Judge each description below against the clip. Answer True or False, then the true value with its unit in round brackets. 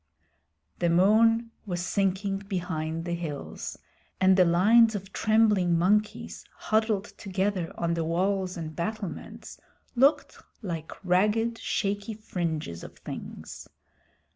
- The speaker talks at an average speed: False (115 wpm)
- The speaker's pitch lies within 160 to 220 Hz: True (190 Hz)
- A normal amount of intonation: True (3.6 semitones)